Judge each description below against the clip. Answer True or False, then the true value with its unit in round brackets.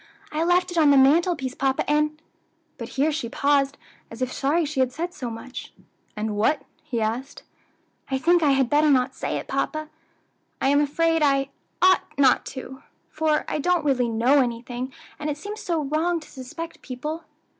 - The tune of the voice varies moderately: True (3.4 semitones)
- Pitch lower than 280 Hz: False (285 Hz)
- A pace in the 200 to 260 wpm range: False (180 wpm)